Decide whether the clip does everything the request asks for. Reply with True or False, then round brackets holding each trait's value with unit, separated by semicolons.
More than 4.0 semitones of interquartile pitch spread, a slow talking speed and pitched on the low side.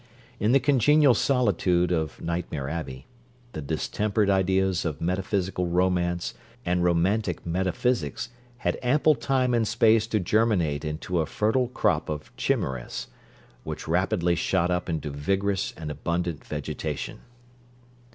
True (4.5 semitones; 125 wpm; 90 Hz)